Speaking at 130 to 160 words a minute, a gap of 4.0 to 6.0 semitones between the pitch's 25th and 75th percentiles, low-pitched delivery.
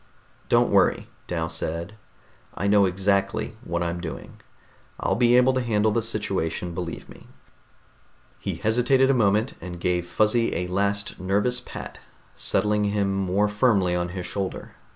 No: average, 150 wpm; average, 3.4 semitones; low, 100 Hz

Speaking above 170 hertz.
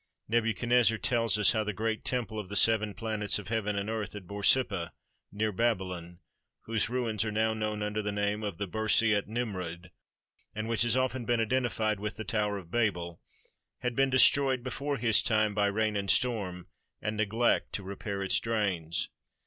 No: low, 110 Hz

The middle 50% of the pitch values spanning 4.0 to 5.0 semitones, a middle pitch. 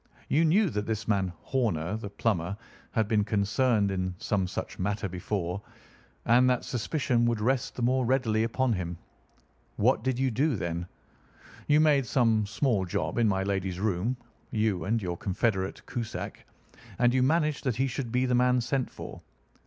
No: average, 4.4 semitones; low, 115 Hz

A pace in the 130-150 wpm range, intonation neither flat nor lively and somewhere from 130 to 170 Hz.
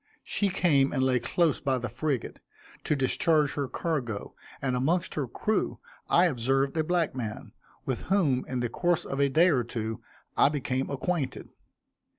No: average, 165 wpm; average, 4.3 semitones; low, 135 Hz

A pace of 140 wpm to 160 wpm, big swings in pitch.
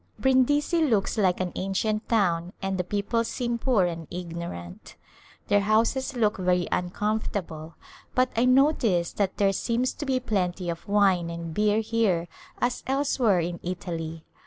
No: average, 150 wpm; average, 4.9 semitones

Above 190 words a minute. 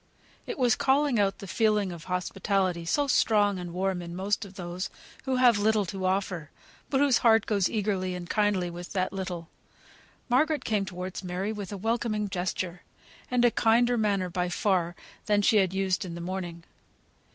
No: average, 180 wpm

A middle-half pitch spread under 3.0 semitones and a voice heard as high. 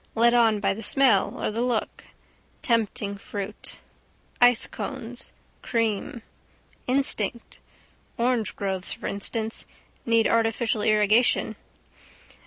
Yes: narrow, 2.4 semitones; high, 225 Hz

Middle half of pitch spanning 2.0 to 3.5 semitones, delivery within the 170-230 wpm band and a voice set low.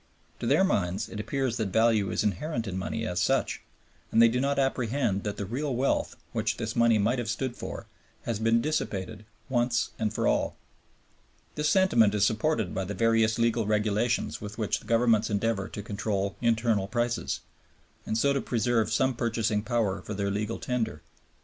Yes: narrow, 2.5 semitones; average, 180 wpm; low, 115 Hz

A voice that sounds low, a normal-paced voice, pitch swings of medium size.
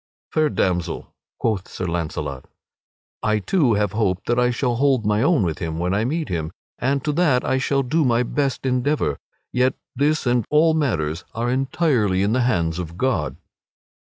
No: low, 120 Hz; average, 180 wpm; wide, 6.8 semitones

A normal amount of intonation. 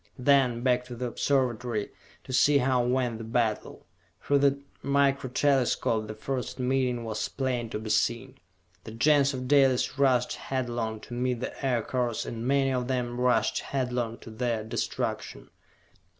No: narrow, 2.3 semitones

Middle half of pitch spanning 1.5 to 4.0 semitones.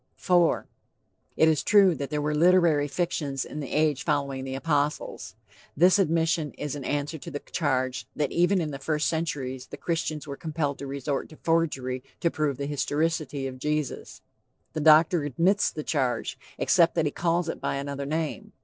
Yes: average, 2.8 semitones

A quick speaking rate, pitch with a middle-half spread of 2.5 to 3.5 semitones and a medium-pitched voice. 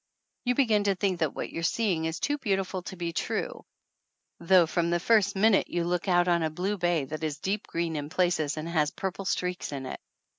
Yes: fast, 220 wpm; average, 3.2 semitones; medium, 175 Hz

